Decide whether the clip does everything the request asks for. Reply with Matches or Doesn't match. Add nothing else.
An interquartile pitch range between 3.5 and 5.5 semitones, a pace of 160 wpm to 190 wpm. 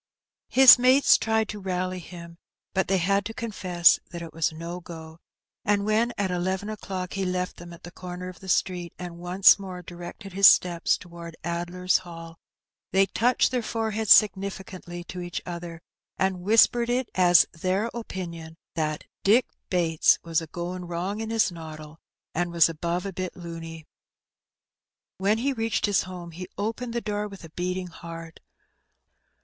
Doesn't match